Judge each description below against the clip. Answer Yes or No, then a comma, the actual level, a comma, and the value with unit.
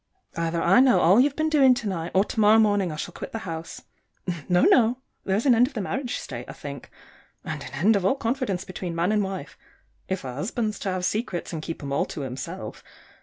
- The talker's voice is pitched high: Yes, high, 195 Hz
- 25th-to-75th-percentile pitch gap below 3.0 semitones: No, wide, 5.5 semitones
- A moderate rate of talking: No, fast, 230 wpm